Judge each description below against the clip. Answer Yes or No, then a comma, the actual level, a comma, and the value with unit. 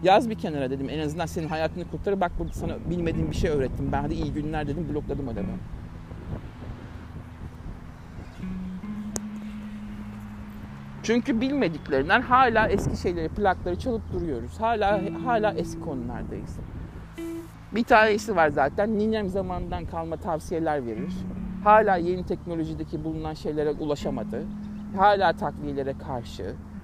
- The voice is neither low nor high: Yes, medium, 160 Hz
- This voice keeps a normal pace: Yes, average, 120 wpm